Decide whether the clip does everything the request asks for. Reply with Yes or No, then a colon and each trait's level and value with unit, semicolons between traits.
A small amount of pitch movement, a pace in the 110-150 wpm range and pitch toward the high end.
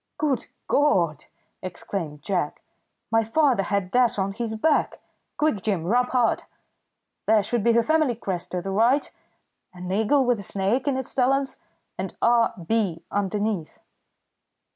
No: average, 4.5 semitones; average, 145 wpm; high, 220 Hz